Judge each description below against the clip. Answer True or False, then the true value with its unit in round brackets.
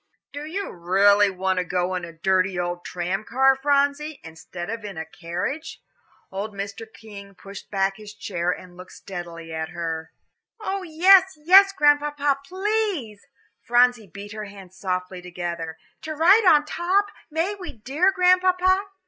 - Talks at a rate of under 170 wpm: True (155 wpm)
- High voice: True (210 Hz)